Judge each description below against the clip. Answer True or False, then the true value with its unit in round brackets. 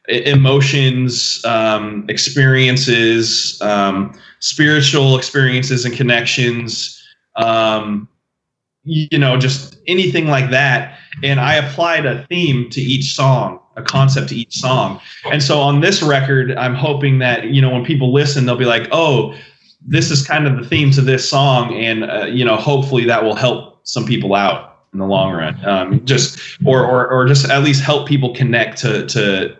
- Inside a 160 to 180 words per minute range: True (165 wpm)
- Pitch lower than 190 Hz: True (135 Hz)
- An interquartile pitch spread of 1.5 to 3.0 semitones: True (2.6 semitones)